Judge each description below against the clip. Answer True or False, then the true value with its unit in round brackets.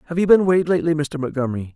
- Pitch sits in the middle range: True (155 Hz)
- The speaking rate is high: True (240 wpm)